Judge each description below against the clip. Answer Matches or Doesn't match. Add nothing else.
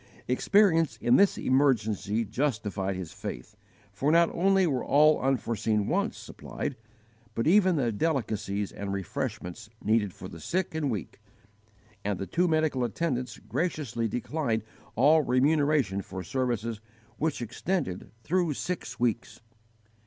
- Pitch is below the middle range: Matches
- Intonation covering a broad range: Matches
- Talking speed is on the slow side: Matches